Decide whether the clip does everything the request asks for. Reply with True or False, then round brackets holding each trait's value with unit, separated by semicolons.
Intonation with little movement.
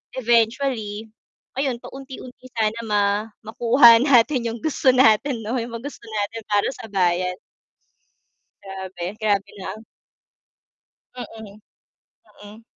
False (3.2 semitones)